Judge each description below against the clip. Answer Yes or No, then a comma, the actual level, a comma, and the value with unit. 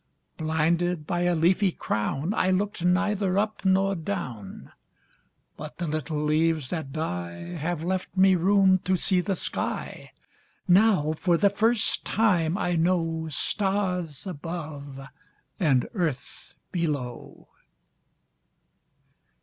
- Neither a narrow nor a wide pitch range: Yes, average, 3.4 semitones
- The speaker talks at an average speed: No, slow, 100 wpm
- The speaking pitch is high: No, medium, 175 Hz